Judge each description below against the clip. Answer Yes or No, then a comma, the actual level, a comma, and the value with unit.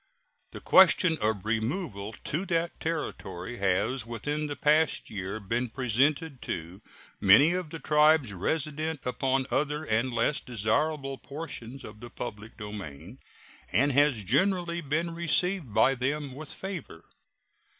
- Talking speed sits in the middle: No, slow, 130 wpm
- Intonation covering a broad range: Yes, wide, 6.0 semitones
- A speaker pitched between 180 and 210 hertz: No, low, 135 Hz